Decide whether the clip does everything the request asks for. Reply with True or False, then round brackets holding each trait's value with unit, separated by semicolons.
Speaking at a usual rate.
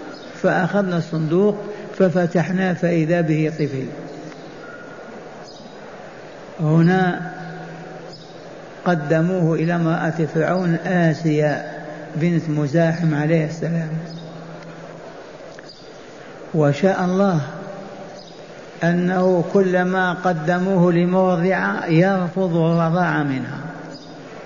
False (60 wpm)